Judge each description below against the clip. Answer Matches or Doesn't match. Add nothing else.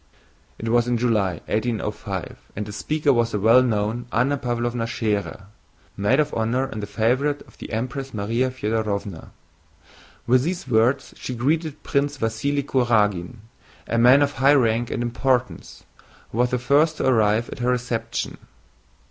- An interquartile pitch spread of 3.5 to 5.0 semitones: Doesn't match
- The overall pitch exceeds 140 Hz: Doesn't match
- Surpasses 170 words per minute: Doesn't match